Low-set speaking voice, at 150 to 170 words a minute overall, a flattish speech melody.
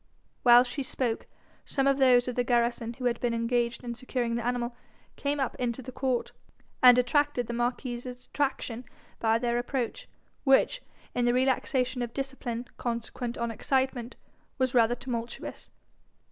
No: high, 245 Hz; average, 155 wpm; narrow, 1.6 semitones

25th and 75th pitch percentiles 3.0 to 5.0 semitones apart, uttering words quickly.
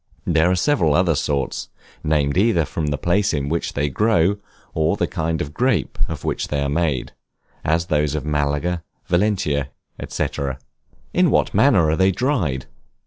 No: average, 3.8 semitones; average, 165 wpm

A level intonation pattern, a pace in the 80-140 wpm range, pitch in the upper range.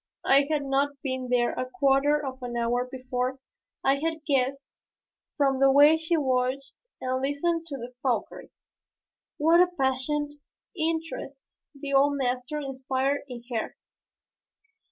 Yes: narrow, 2.3 semitones; slow, 135 wpm; very high, 275 Hz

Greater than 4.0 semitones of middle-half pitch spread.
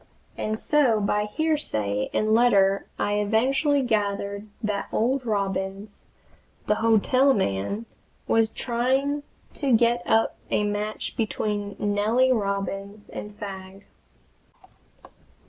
No: average, 3.1 semitones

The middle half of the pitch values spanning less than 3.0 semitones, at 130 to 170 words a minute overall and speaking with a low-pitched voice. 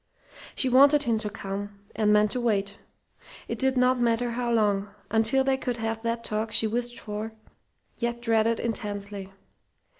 No: narrow, 2.4 semitones; average, 160 wpm; high, 225 Hz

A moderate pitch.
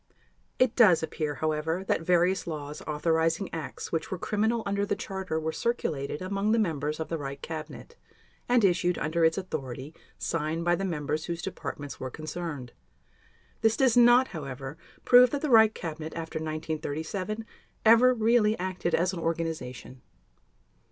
Yes: medium, 165 Hz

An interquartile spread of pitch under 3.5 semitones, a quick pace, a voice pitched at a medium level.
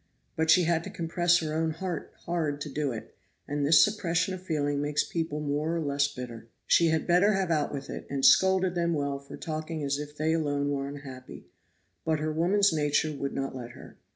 Yes: average, 2.9 semitones; fast, 210 wpm; medium, 155 Hz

